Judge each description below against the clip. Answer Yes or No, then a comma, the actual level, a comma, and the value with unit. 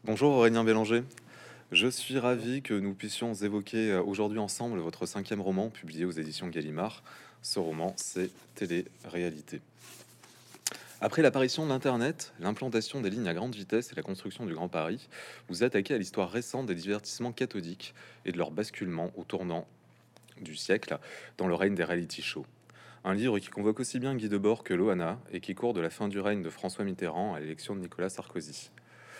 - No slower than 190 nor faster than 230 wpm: No, average, 180 wpm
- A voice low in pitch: Yes, low, 105 Hz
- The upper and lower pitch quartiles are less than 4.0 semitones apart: No, average, 4.7 semitones